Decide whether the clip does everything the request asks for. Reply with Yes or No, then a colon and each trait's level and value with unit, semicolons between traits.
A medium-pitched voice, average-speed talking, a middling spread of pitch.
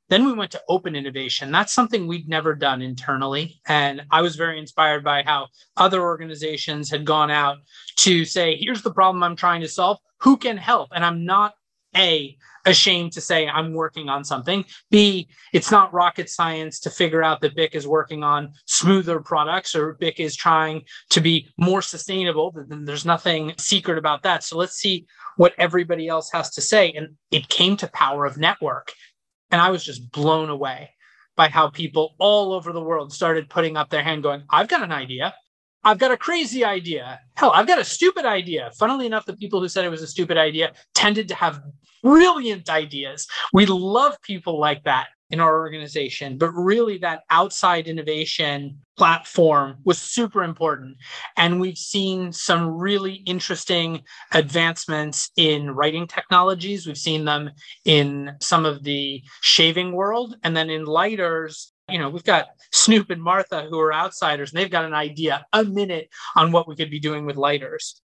Yes: medium, 165 Hz; average, 180 wpm; average, 3.5 semitones